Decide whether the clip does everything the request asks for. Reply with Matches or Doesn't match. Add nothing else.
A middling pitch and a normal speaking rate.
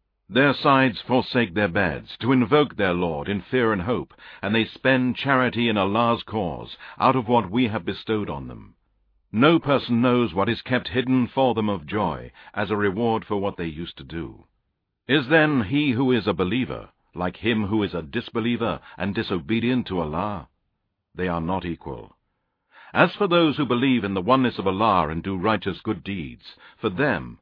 Doesn't match